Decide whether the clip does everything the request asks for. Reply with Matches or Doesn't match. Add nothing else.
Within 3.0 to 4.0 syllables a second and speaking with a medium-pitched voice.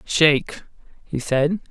Matches